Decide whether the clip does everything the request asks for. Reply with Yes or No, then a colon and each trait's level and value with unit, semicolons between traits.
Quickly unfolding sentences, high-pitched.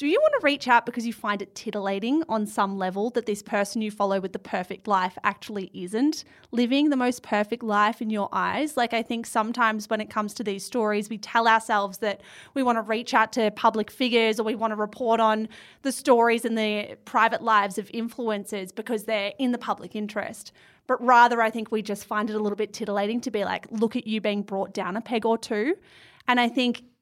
Yes: fast, 230 wpm; high, 220 Hz